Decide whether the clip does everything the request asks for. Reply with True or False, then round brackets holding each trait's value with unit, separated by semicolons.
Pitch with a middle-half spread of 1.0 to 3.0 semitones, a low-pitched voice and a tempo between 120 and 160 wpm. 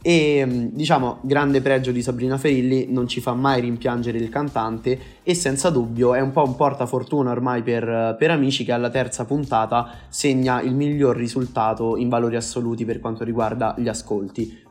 False (2.4 semitones; 125 Hz; 170 wpm)